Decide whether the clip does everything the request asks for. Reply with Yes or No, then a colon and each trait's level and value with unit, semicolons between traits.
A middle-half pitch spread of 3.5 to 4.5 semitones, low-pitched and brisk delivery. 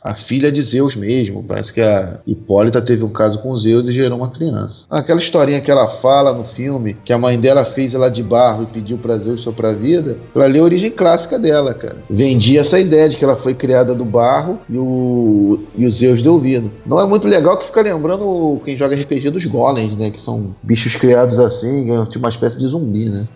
Yes: average, 3.8 semitones; low, 125 Hz; fast, 225 wpm